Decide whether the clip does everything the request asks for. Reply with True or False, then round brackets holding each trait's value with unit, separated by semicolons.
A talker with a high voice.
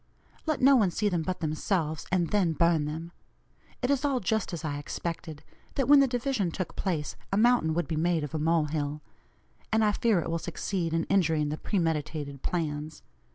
False (170 Hz)